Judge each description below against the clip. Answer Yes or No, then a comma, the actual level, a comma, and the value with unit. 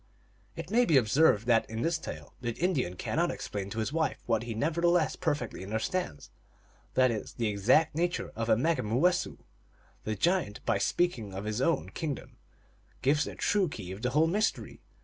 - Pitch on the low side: Yes, low, 130 Hz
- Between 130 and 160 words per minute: No, average, 185 wpm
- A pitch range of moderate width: No, wide, 7.2 semitones